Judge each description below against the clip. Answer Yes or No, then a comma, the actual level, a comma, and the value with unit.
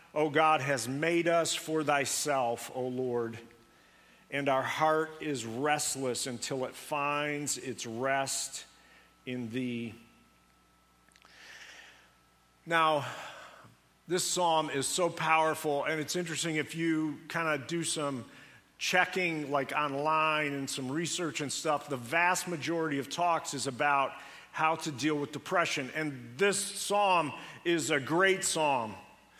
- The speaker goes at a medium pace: No, slow, 130 wpm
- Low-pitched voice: No, medium, 150 Hz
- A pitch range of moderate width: Yes, average, 3.4 semitones